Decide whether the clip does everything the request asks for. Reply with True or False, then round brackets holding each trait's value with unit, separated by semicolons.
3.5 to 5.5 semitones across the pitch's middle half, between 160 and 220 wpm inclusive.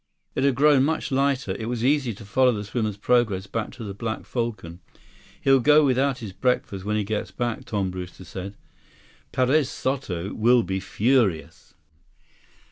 True (5.0 semitones; 165 wpm)